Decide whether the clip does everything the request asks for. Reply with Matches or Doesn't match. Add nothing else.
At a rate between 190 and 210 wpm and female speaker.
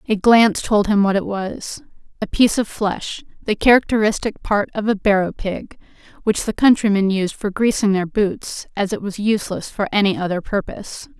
Doesn't match